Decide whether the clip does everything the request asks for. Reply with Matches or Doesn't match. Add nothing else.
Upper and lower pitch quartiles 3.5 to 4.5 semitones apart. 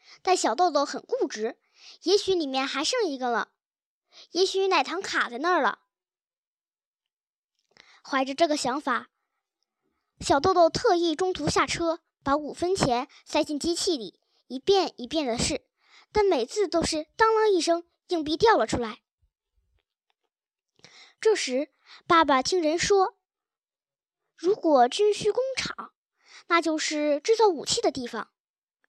Doesn't match